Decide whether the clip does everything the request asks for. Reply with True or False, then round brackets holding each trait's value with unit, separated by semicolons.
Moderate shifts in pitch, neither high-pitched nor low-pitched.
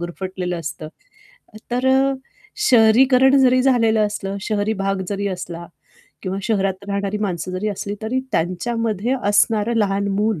False (3.1 semitones; 205 Hz)